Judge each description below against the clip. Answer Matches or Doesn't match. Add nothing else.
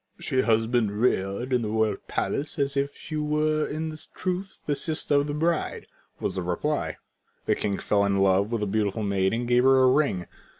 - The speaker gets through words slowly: Doesn't match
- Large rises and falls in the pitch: Matches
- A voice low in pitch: Matches